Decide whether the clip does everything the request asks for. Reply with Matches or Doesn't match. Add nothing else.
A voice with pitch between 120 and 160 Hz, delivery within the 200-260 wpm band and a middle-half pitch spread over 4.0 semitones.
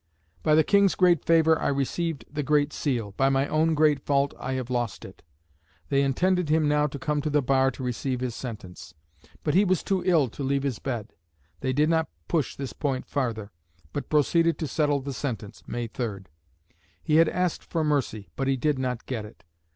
Doesn't match